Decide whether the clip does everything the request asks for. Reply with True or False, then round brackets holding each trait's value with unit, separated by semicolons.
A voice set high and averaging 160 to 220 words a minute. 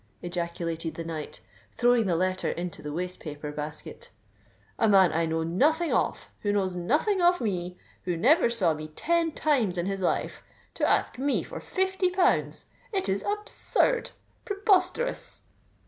False (195 Hz; 140 wpm)